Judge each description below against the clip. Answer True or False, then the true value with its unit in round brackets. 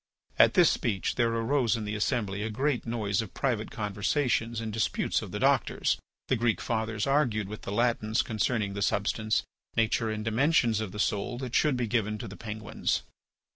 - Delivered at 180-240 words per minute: True (185 wpm)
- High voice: False (110 Hz)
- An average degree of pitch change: False (2.2 semitones)